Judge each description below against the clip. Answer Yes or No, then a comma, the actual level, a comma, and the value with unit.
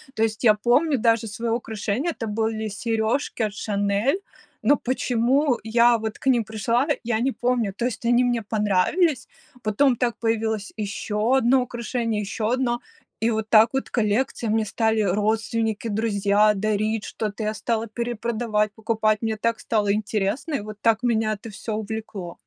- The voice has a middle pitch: No, high, 225 Hz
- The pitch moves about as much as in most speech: No, narrow, 2.0 semitones